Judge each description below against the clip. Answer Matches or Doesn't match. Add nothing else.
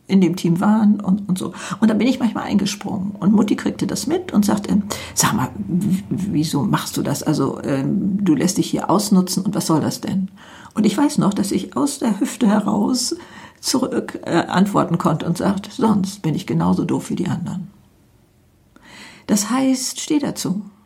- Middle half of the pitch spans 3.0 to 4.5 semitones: Matches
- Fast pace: Matches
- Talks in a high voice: Matches